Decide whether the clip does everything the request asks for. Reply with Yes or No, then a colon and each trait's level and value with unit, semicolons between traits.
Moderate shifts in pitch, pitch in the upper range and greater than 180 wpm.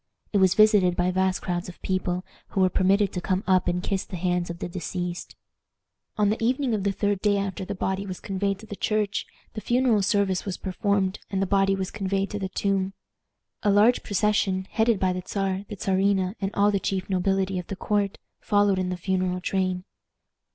No: narrow, 1.6 semitones; high, 195 Hz; fast, 205 wpm